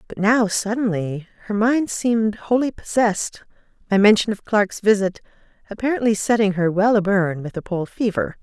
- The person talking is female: Yes, female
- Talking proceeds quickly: No, average, 165 wpm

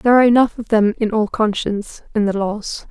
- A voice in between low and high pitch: No, high, 220 Hz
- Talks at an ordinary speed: No, fast, 225 wpm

